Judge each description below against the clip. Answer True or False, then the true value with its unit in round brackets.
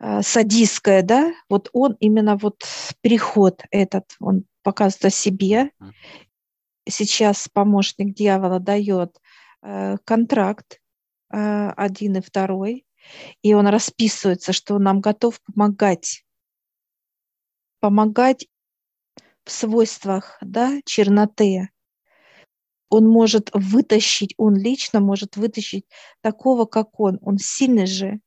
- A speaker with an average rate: False (100 wpm)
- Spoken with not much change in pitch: True (2.1 semitones)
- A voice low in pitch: False (205 Hz)